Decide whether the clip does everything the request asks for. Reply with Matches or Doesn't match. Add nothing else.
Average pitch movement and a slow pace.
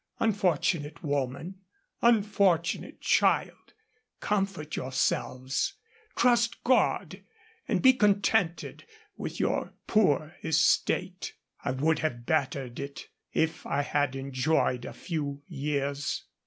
Doesn't match